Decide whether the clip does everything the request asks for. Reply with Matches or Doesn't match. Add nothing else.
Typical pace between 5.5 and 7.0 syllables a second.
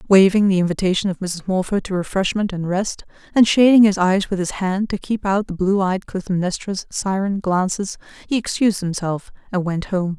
Doesn't match